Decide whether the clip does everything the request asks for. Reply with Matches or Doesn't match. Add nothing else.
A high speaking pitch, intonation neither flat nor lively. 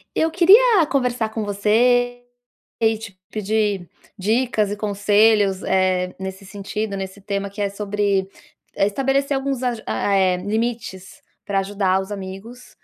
Matches